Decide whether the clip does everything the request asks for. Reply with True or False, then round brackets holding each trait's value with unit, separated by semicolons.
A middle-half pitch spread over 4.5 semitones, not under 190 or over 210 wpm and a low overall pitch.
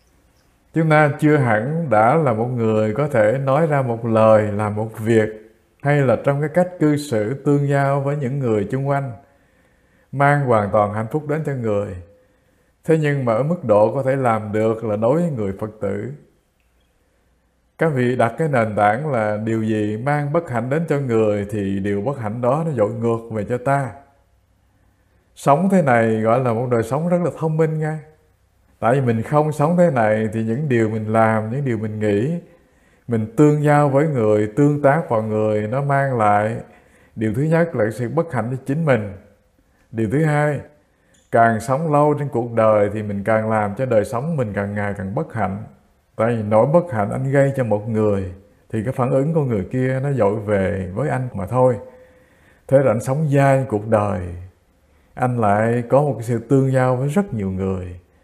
True (5.0 semitones; 200 wpm; 115 Hz)